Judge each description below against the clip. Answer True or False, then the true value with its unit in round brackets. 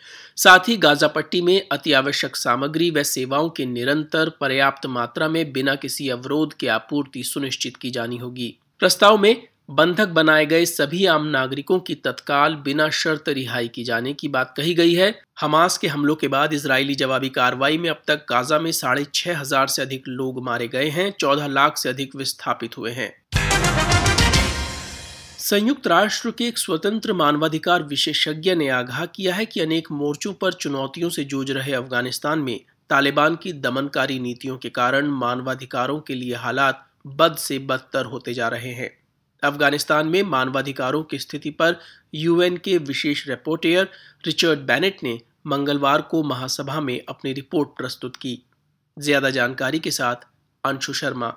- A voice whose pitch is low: False (145 Hz)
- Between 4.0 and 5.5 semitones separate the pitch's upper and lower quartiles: False (3.5 semitones)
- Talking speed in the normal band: True (160 wpm)